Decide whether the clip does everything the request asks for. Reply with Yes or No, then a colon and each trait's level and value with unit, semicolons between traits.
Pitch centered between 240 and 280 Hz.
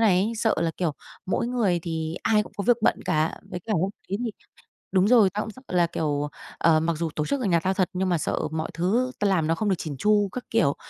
No: medium, 185 Hz